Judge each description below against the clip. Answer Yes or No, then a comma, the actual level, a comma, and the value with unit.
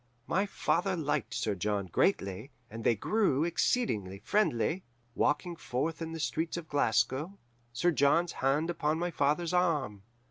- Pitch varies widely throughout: Yes, wide, 6.5 semitones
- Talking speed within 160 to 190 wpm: No, average, 145 wpm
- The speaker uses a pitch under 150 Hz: No, medium, 155 Hz